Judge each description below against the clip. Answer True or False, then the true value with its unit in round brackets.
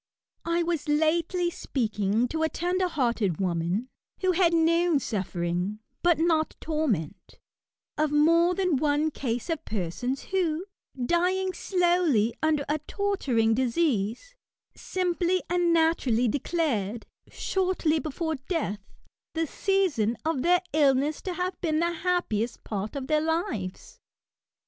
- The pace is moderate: False (125 wpm)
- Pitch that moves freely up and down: True (6.7 semitones)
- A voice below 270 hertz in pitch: False (315 Hz)